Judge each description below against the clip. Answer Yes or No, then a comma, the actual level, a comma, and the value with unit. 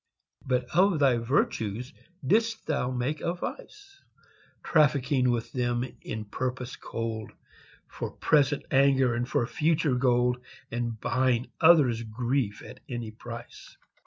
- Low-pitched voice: Yes, low, 125 Hz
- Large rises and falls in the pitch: No, average, 3.5 semitones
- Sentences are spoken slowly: Yes, slow, 130 wpm